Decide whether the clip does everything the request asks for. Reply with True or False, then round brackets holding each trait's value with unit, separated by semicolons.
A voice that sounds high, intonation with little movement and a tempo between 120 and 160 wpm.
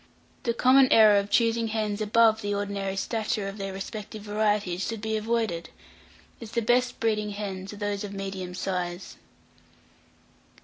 True (210 Hz; 2.2 semitones; 150 wpm)